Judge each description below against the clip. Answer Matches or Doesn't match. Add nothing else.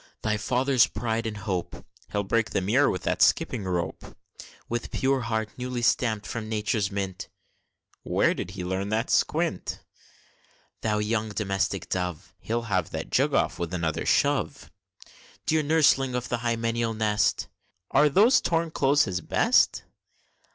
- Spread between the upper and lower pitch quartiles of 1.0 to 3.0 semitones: Doesn't match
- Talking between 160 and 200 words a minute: Doesn't match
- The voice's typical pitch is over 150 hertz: Doesn't match